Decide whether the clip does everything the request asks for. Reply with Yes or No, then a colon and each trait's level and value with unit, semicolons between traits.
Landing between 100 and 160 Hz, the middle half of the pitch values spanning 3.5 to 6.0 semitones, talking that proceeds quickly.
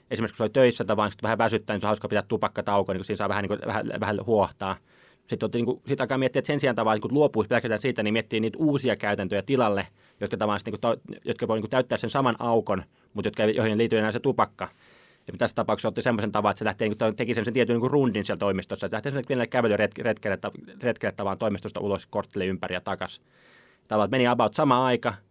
No: low, 110 Hz; average, 2.9 semitones; fast, 220 wpm